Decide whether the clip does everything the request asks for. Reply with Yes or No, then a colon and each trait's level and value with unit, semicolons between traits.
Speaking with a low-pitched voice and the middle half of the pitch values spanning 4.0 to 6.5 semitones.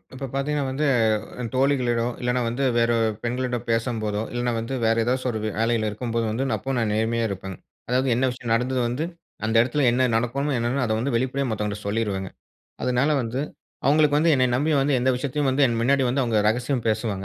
No: low, 125 Hz; average, 2.7 semitones